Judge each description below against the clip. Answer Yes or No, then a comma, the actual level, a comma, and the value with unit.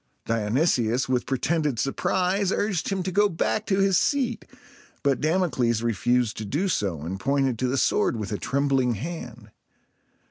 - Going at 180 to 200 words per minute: No, average, 155 wpm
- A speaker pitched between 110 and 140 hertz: Yes, low, 135 Hz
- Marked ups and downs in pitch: Yes, wide, 7.5 semitones